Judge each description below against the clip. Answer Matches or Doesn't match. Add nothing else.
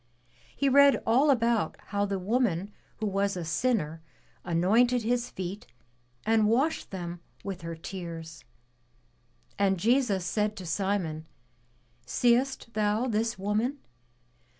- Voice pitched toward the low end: Doesn't match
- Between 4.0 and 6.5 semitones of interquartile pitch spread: Matches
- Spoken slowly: Matches